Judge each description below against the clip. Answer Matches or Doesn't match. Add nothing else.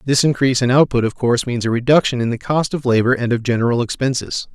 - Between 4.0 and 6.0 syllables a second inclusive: Doesn't match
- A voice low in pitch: Matches